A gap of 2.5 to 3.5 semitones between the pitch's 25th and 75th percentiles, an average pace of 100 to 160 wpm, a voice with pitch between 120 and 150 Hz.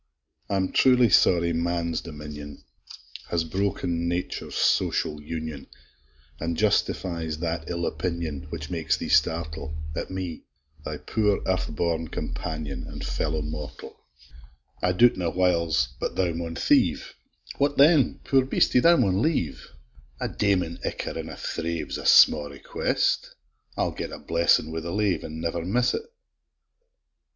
No: average, 3.0 semitones; average, 140 wpm; very low, 85 Hz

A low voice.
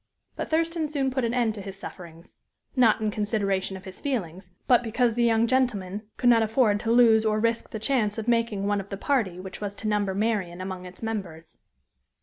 No: high, 215 Hz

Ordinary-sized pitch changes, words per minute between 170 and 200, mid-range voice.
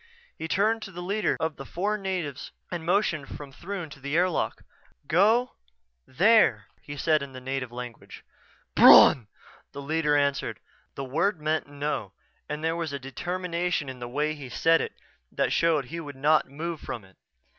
Yes: average, 4.2 semitones; average, 175 wpm; medium, 155 Hz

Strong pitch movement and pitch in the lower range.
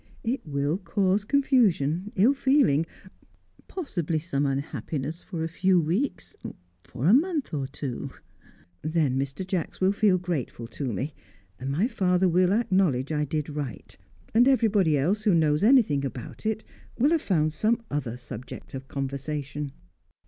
No: wide, 6.6 semitones; medium, 165 Hz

